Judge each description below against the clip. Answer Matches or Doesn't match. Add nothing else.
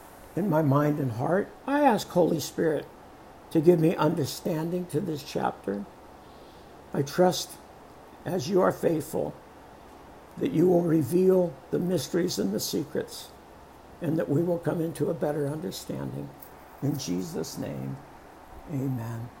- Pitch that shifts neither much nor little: Matches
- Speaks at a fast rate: Doesn't match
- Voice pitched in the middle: Matches